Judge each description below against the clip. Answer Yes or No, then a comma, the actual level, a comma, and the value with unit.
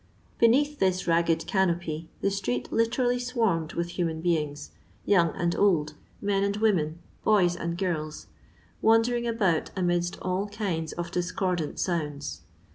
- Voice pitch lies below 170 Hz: No, medium, 180 Hz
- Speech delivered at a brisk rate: No, slow, 135 wpm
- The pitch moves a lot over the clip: No, average, 3.8 semitones